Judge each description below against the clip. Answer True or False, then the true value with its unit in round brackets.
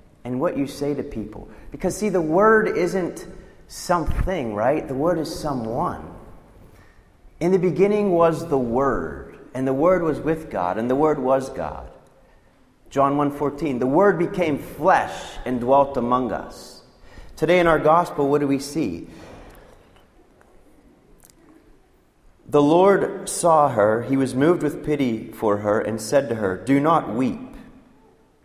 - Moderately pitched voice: True (145 Hz)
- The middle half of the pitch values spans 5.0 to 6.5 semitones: True (5.6 semitones)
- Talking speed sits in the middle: True (150 wpm)